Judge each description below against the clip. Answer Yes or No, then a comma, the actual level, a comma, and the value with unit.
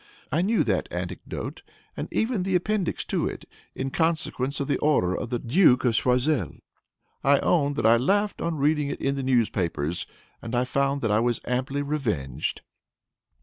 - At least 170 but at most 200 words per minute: Yes, average, 175 wpm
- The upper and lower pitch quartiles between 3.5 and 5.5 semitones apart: Yes, average, 4.7 semitones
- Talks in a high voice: No, low, 135 Hz